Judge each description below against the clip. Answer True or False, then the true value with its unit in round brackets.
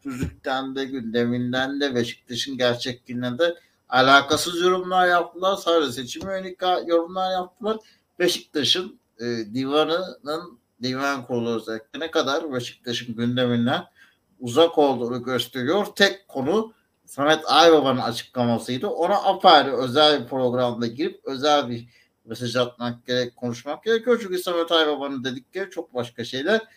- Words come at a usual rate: True (120 wpm)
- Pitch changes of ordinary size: False (6.1 semitones)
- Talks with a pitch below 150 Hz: True (135 Hz)